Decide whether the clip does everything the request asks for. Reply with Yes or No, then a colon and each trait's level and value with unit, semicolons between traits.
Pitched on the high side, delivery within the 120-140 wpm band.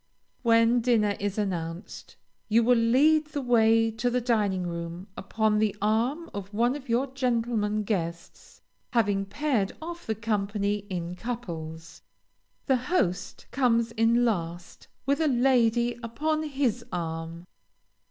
Yes: high, 225 Hz; slow, 135 wpm